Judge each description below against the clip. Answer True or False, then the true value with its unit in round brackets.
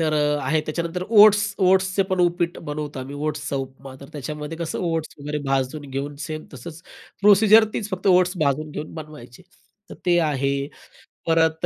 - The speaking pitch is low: False (155 Hz)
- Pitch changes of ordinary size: True (3.8 semitones)